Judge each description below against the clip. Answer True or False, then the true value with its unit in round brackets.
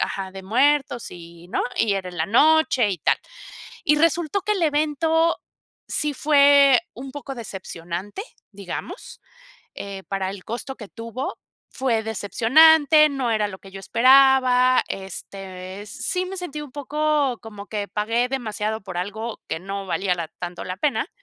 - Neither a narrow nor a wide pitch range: False (6.8 semitones)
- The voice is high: True (230 Hz)